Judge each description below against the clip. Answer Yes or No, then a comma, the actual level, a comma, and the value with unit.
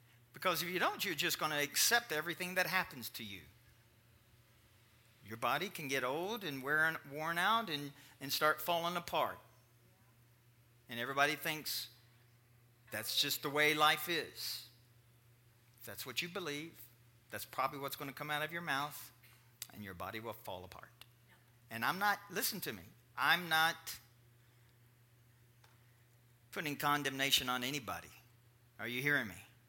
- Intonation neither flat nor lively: Yes, average, 3.8 semitones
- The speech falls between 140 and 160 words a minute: Yes, average, 150 wpm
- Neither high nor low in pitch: No, low, 120 Hz